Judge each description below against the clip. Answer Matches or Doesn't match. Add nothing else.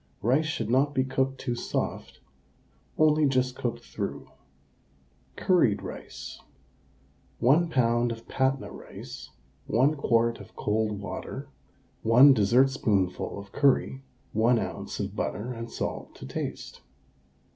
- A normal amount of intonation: Matches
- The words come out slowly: Matches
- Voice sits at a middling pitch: Doesn't match